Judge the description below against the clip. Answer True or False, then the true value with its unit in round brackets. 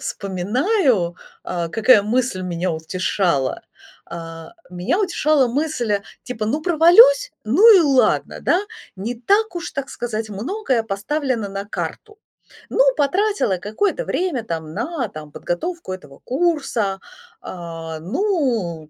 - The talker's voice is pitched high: True (230 Hz)